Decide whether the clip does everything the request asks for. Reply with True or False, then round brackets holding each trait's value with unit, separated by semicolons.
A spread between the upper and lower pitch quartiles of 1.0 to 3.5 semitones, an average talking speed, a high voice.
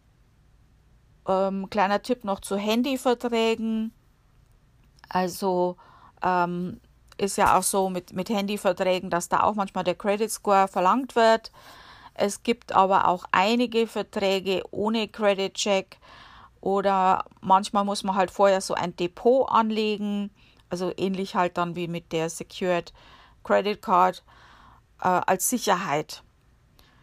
False (2.5 semitones; 120 wpm; 195 Hz)